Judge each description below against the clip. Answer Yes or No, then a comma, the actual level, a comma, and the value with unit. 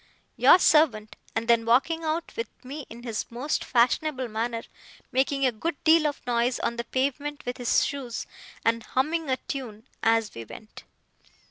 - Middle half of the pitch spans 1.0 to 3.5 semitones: No, average, 4.1 semitones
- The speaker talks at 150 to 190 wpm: Yes, average, 165 wpm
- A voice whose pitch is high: Yes, very high, 250 Hz